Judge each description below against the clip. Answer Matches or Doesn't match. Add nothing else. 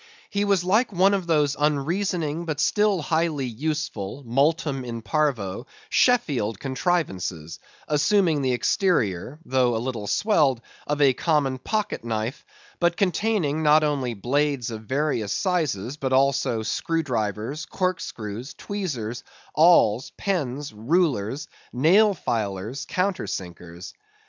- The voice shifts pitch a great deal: Matches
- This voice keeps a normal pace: Doesn't match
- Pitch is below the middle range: Doesn't match